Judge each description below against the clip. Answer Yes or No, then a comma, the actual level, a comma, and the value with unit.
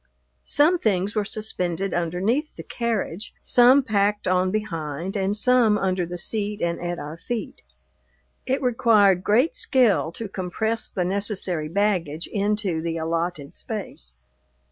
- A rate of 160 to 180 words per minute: No, slow, 135 wpm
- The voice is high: Yes, high, 200 Hz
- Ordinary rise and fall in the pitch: Yes, average, 4.0 semitones